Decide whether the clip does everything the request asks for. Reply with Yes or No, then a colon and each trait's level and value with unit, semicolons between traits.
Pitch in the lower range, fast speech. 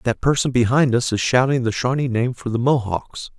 Yes: low, 125 Hz; fast, 215 wpm